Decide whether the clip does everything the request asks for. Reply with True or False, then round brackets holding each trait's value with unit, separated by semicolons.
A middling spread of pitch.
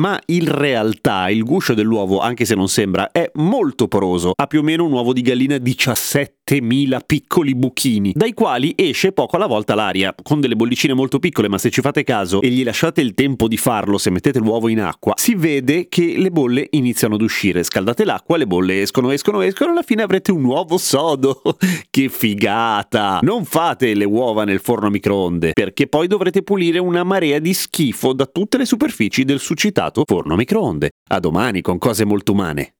False (7.4 semitones)